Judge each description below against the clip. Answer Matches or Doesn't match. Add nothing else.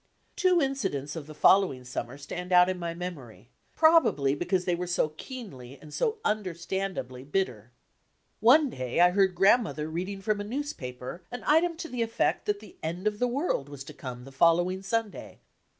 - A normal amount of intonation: Doesn't match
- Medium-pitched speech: Matches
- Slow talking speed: Doesn't match